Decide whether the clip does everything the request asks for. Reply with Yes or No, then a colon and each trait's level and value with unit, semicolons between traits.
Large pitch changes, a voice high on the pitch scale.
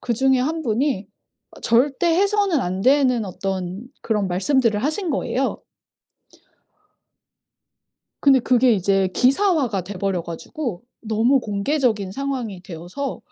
Yes: wide, 6.1 semitones; high, 240 Hz